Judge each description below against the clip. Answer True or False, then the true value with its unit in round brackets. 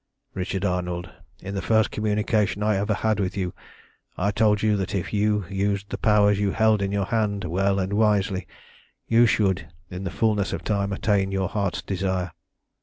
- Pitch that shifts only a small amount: True (1.7 semitones)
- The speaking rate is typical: True (185 wpm)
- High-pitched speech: False (100 Hz)